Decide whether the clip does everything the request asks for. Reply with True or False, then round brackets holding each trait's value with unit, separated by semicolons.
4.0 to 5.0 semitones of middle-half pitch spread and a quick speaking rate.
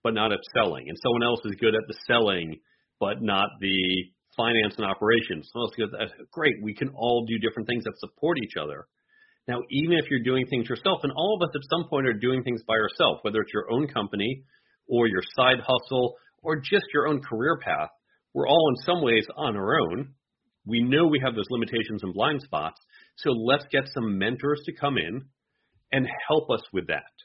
True (4.3 semitones; 215 wpm)